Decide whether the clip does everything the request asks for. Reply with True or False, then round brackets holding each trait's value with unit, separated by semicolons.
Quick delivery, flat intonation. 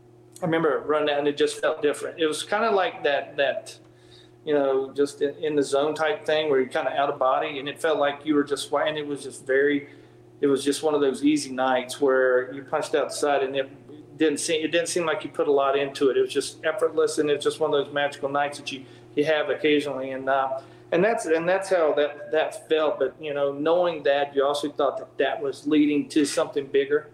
True (250 wpm; 2.2 semitones)